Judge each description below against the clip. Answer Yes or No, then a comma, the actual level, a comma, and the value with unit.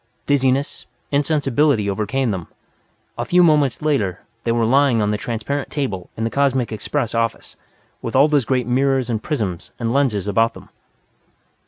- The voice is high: No, low, 125 Hz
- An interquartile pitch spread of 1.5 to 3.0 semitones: No, average, 4.1 semitones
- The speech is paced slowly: No, average, 160 wpm